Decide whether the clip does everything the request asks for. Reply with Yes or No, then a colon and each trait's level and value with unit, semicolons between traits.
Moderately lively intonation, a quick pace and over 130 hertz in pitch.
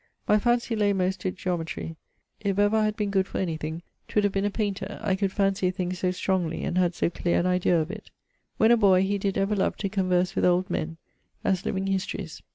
No: narrow, 2.1 semitones; fast, 235 wpm; high, 190 Hz